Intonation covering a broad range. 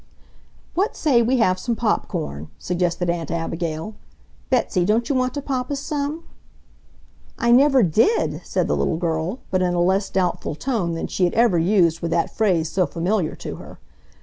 Yes: wide, 6.3 semitones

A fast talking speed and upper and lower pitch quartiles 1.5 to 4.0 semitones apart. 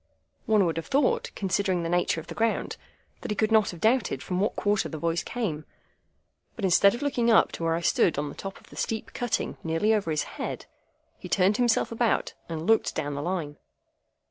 No: fast, 215 wpm; average, 5.1 semitones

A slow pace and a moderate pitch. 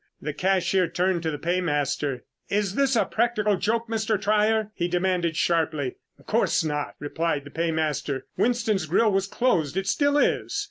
No: average, 165 wpm; medium, 180 Hz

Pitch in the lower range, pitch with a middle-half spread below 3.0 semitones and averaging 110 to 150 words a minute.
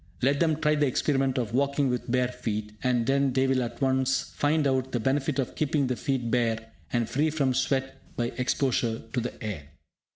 No: low, 130 Hz; narrow, 2.4 semitones; average, 200 wpm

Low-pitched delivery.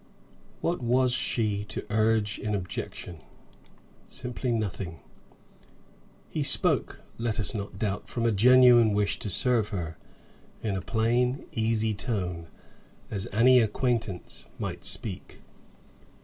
Yes: low, 110 Hz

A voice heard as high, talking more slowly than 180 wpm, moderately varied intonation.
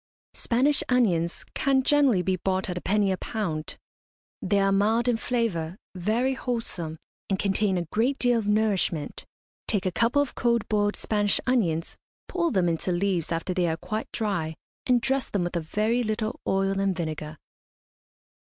Yes: high, 205 Hz; average, 170 wpm; average, 4.9 semitones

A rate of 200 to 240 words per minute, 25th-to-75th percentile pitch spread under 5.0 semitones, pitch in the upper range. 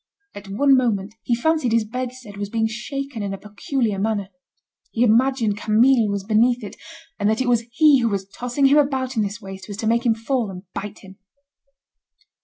Yes: fast, 205 wpm; average, 3.8 semitones; high, 225 Hz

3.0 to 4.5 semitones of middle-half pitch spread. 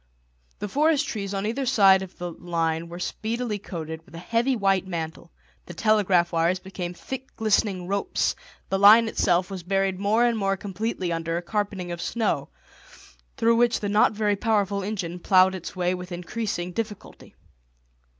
Yes: average, 3.6 semitones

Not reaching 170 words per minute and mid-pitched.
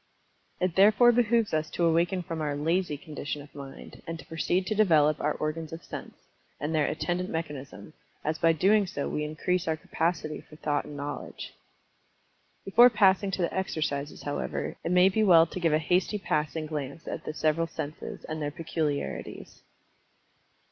No: average, 175 wpm; medium, 160 Hz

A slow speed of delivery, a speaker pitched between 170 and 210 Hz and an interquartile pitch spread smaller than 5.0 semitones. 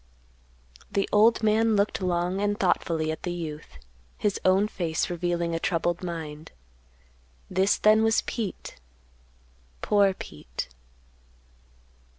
Yes: slow, 115 wpm; medium, 185 Hz; average, 3.4 semitones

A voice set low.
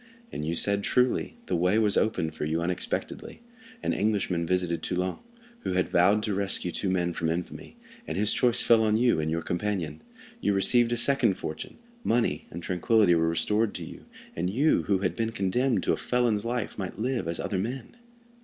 Yes: low, 100 Hz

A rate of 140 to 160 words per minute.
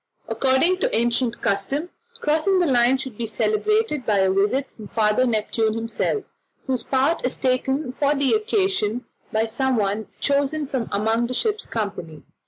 Yes: average, 155 wpm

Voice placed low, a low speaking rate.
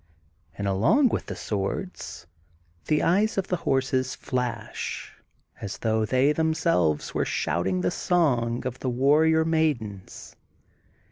Yes: low, 130 Hz; slow, 125 wpm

